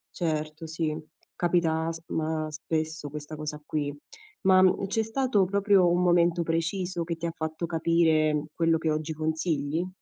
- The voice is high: No, medium, 165 Hz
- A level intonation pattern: Yes, narrow, 2.0 semitones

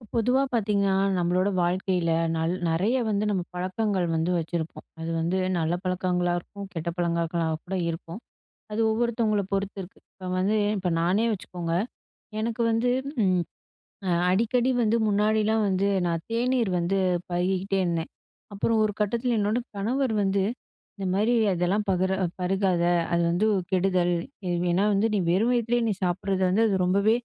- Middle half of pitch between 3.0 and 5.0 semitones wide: Yes, average, 3.4 semitones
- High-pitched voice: Yes, high, 195 Hz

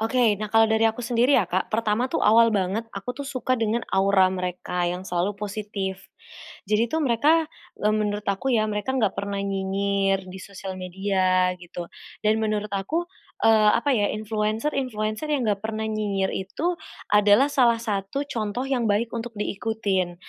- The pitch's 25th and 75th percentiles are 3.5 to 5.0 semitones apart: No, average, 2.8 semitones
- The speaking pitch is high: Yes, high, 210 Hz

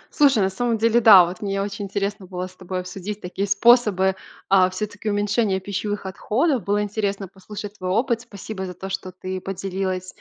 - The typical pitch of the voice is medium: No, high, 200 Hz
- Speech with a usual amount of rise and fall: No, narrow, 2.1 semitones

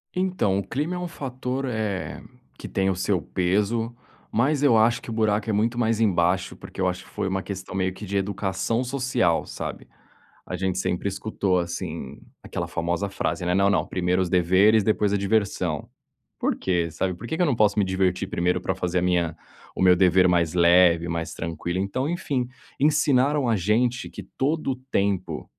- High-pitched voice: No, low, 100 Hz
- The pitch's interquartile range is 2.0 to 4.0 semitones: No, average, 4.5 semitones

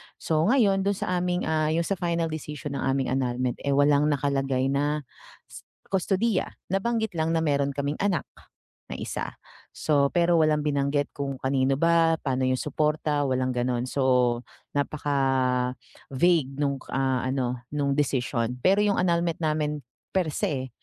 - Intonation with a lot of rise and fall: No, average, 3.7 semitones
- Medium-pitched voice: Yes, medium, 145 Hz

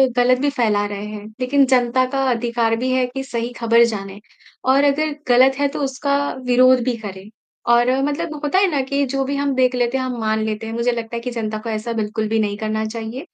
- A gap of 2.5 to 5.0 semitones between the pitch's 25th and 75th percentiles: Yes, average, 3.2 semitones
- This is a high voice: Yes, high, 245 Hz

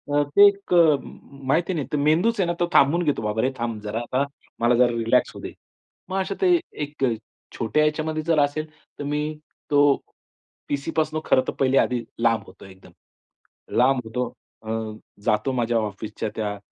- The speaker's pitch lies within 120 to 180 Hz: Yes, medium, 140 Hz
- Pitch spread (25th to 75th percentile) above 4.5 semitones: Yes, average, 5.2 semitones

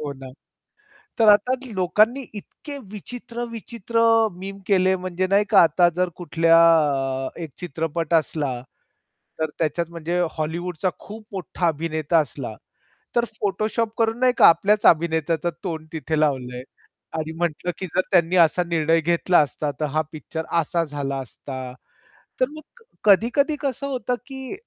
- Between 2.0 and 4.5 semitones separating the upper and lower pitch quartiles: No, average, 5.1 semitones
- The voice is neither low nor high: Yes, medium, 175 Hz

